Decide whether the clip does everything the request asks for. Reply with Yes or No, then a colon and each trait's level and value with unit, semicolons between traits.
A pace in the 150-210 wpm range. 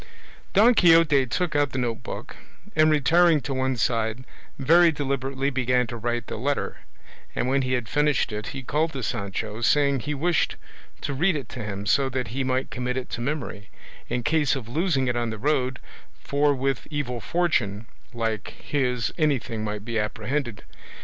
Yes: average, 180 wpm